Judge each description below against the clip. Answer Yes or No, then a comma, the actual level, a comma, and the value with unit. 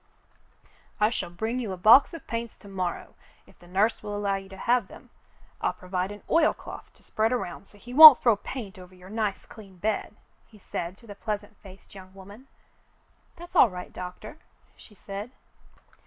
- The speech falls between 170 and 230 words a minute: Yes, average, 185 wpm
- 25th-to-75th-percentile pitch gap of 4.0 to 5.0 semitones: No, average, 3.5 semitones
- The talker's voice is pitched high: Yes, high, 205 Hz